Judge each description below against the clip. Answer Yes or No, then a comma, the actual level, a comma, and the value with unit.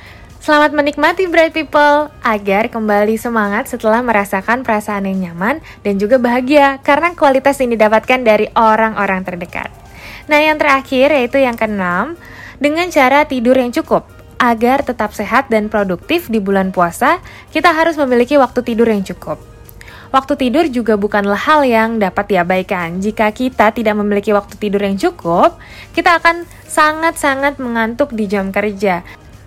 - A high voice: Yes, high, 230 Hz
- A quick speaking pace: Yes, fast, 145 wpm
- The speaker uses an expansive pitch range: Yes, wide, 5.9 semitones